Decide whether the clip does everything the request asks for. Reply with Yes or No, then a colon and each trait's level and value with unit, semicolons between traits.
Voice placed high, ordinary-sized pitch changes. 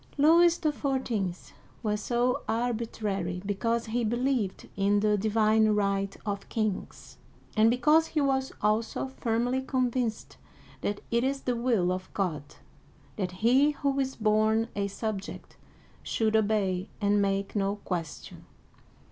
Yes: high, 220 Hz; average, 3.7 semitones